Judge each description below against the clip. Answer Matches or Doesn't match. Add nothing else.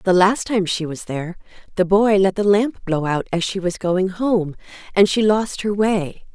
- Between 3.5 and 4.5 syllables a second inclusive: Matches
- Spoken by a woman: Matches